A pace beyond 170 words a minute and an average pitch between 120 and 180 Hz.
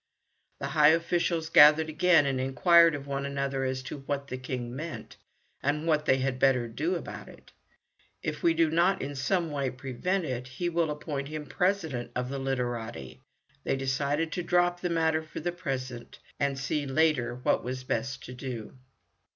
Yes: average, 185 wpm; medium, 140 Hz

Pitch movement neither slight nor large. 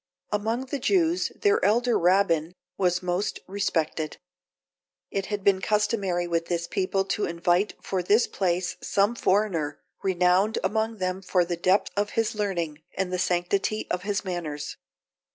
Yes: average, 3.0 semitones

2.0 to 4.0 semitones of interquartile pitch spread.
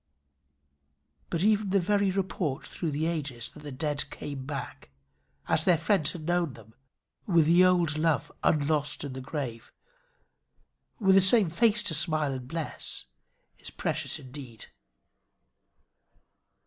No: average, 4.4 semitones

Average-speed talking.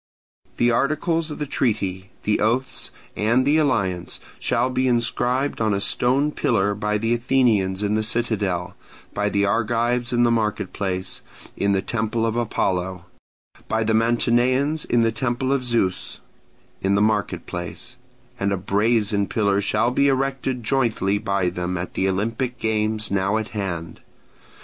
Yes: average, 155 wpm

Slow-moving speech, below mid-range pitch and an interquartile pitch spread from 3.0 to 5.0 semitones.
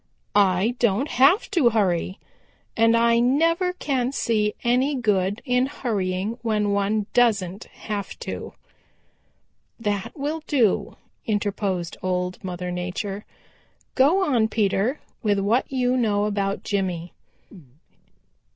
No: slow, 115 wpm; high, 215 Hz; average, 4.1 semitones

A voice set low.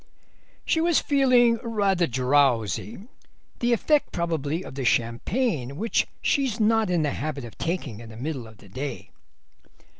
No: medium, 165 Hz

